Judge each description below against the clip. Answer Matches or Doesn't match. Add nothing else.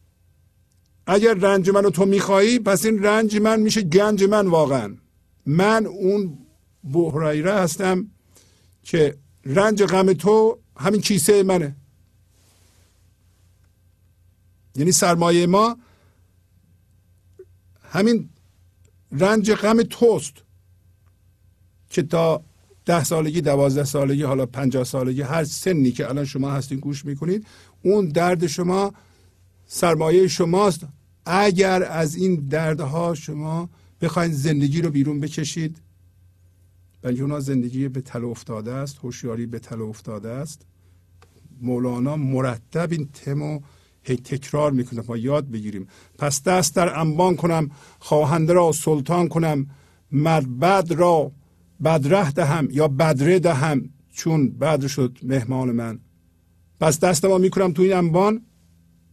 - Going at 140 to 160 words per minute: Doesn't match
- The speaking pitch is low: Doesn't match